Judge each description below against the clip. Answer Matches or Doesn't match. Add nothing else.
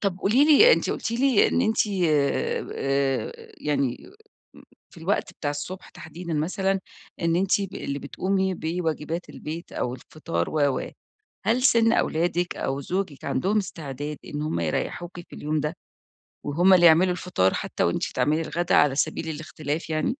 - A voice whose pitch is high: Doesn't match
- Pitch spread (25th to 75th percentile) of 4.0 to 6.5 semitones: Matches